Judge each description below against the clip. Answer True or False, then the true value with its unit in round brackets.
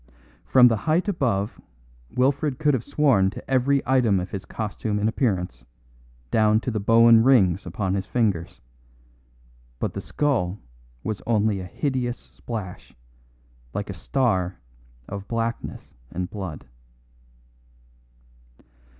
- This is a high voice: False (110 Hz)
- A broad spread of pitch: False (4.9 semitones)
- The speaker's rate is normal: False (125 wpm)